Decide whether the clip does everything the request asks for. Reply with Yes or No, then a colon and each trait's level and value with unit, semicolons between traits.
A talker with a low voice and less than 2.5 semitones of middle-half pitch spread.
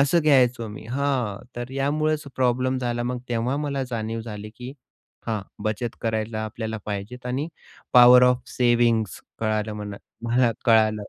No: low, 120 Hz; average, 2.8 semitones